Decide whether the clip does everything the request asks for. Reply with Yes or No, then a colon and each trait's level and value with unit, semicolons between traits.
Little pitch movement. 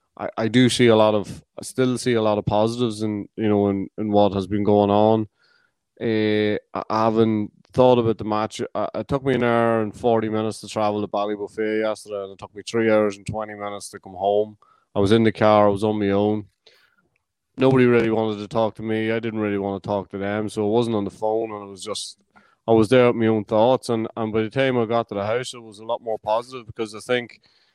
Yes: narrow, 1.6 semitones